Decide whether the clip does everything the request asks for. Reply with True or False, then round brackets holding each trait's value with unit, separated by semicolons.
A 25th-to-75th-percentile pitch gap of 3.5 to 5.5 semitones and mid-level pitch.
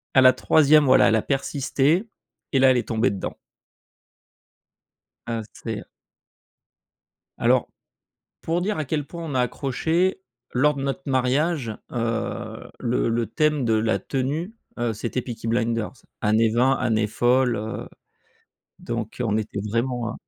False (4.1 semitones; 125 Hz)